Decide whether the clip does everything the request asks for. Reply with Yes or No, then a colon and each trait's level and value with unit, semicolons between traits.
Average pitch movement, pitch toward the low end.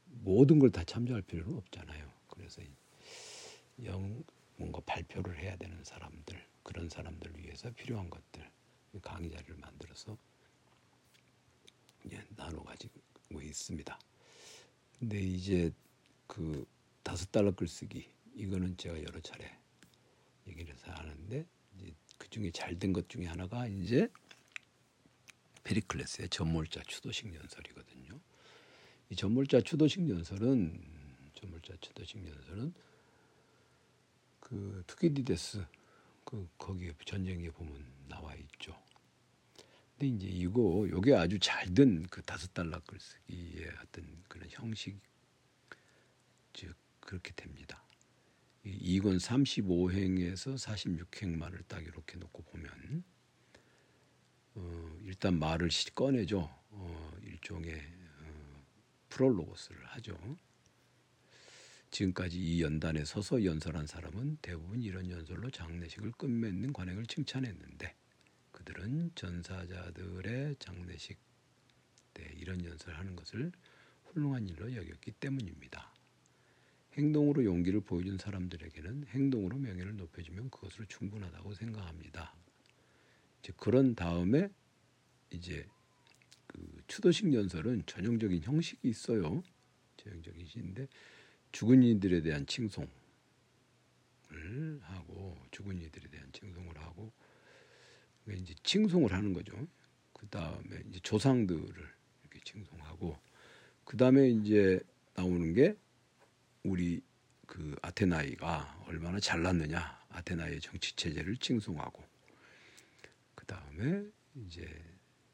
Yes: average, 4.8 semitones; very low, 95 Hz